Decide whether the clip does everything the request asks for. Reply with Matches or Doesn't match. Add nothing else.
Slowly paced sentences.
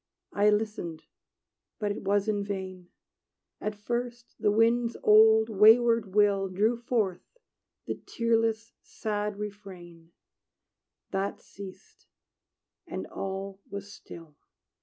Matches